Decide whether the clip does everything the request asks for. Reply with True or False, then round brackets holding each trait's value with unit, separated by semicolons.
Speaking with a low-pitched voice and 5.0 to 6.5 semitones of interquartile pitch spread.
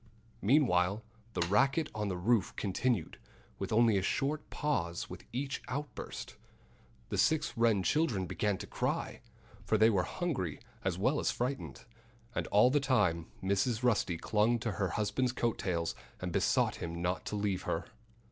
True (105 Hz; 5.5 semitones)